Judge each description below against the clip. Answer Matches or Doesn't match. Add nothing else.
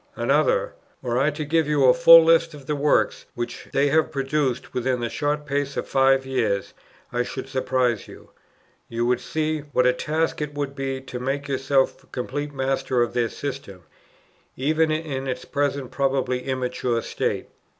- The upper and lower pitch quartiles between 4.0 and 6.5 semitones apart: Doesn't match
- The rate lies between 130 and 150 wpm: Doesn't match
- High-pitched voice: Doesn't match